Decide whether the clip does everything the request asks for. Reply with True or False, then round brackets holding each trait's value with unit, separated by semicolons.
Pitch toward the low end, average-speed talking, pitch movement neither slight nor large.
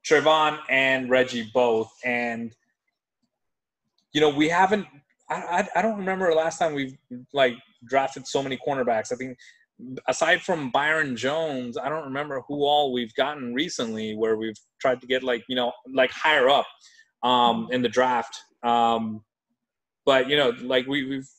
True (130 Hz; 170 wpm; 4.0 semitones)